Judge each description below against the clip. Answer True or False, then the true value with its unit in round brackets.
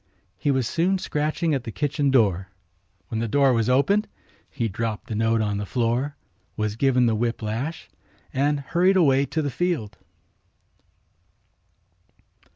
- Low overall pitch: True (130 Hz)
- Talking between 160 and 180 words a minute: False (150 wpm)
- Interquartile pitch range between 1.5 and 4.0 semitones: False (4.6 semitones)